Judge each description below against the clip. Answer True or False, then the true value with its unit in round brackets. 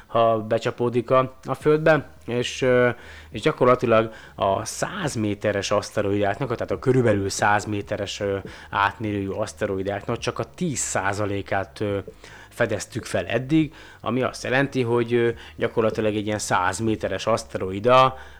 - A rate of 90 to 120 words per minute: True (115 wpm)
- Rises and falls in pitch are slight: False (3.9 semitones)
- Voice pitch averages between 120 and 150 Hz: False (110 Hz)